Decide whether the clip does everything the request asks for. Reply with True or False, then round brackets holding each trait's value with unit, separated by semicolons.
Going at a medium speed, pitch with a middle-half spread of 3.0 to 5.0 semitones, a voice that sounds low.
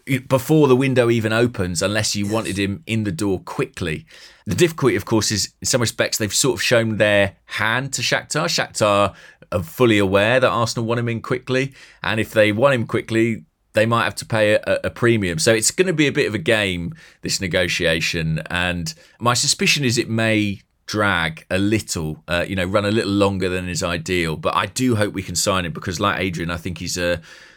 False (215 wpm; 4.2 semitones; 110 Hz)